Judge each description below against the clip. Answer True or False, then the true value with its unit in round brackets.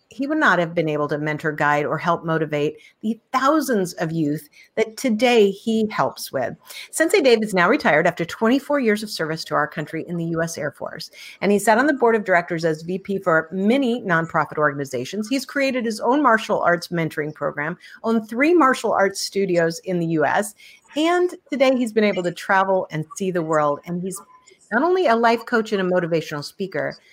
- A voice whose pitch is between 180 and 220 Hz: True (190 Hz)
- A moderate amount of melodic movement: False (6.3 semitones)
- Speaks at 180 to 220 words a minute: True (205 wpm)